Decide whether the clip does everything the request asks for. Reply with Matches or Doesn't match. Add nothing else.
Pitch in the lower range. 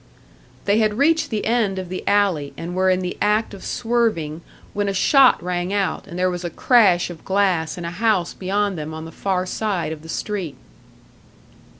Doesn't match